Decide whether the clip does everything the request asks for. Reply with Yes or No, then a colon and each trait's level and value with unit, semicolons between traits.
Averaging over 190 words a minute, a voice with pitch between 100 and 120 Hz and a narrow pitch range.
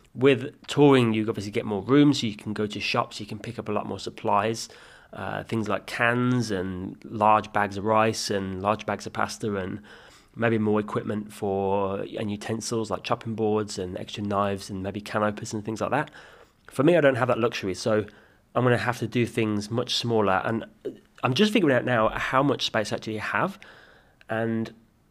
Yes: fast, 205 wpm; low, 110 Hz; narrow, 2.0 semitones